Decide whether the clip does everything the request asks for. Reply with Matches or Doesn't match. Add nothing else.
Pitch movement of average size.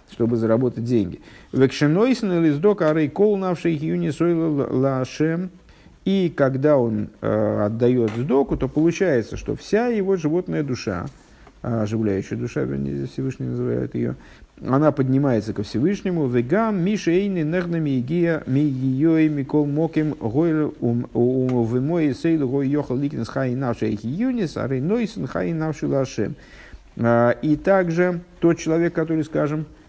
Doesn't match